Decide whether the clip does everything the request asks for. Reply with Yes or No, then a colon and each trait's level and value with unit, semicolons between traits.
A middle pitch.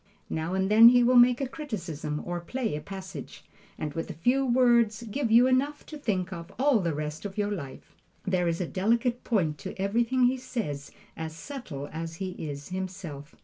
No: high, 195 Hz